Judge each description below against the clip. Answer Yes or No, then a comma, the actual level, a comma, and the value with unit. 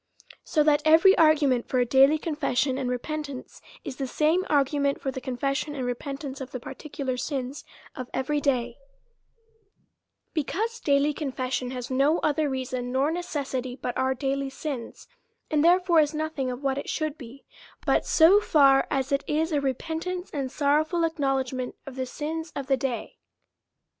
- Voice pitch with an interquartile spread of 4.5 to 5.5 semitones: No, average, 2.9 semitones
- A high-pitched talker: Yes, very high, 280 Hz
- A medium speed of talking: Yes, average, 165 wpm